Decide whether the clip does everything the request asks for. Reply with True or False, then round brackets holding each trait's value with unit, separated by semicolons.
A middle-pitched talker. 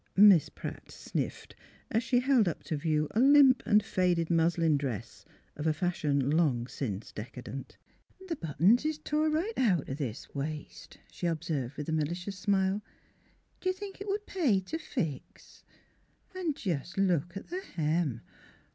True (175 Hz)